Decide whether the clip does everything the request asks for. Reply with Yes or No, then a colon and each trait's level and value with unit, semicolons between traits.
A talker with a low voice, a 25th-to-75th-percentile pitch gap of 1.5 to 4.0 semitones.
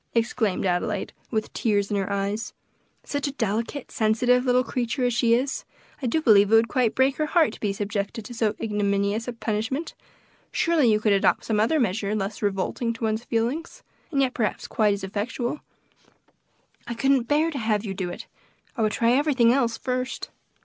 No: high, 230 Hz; average, 3.4 semitones